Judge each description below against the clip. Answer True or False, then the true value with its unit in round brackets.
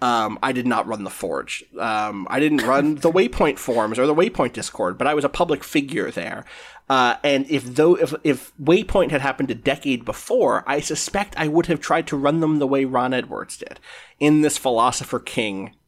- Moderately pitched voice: True (145 Hz)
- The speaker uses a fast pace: True (210 wpm)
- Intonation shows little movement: False (3.9 semitones)